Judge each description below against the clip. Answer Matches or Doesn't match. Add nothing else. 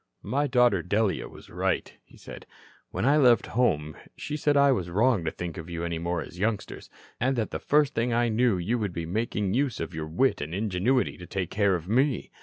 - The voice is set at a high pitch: Doesn't match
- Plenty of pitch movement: Matches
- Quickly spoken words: Matches